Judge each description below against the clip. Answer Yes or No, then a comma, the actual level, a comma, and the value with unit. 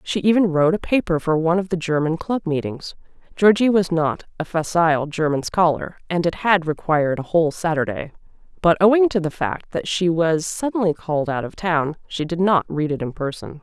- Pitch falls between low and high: Yes, medium, 170 Hz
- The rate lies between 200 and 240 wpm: Yes, fast, 205 wpm